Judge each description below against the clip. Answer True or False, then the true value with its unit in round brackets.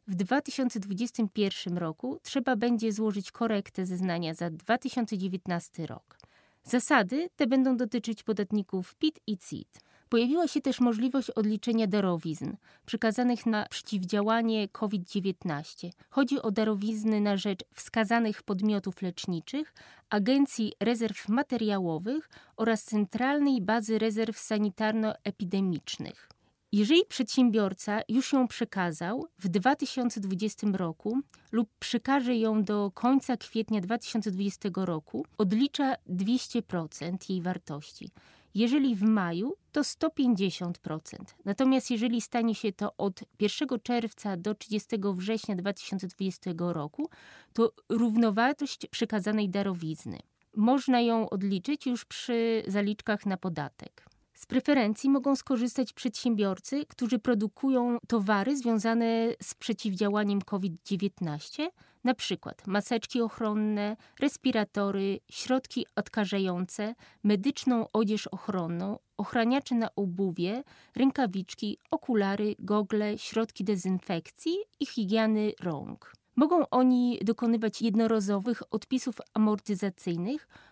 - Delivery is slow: True (100 wpm)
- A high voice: True (220 Hz)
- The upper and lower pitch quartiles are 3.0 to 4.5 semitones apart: True (3.5 semitones)